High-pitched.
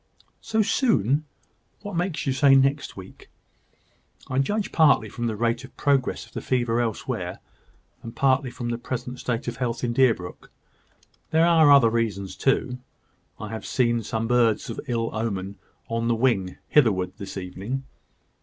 No: low, 120 Hz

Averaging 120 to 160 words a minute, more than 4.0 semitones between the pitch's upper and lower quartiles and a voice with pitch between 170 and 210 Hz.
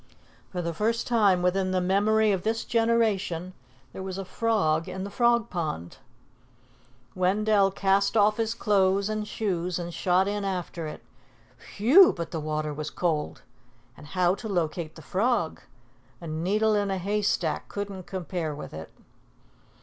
No: average, 155 wpm; average, 3.6 semitones; high, 190 Hz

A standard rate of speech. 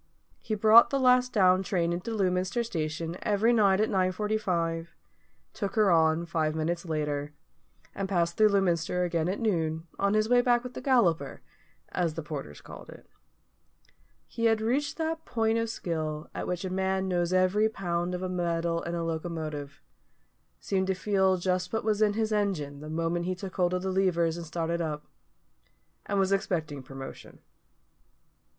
Yes: average, 170 wpm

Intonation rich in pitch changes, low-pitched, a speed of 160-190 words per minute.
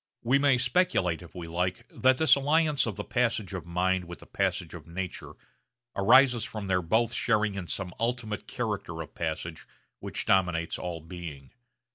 Yes: wide, 5.7 semitones; very low, 95 Hz; average, 170 wpm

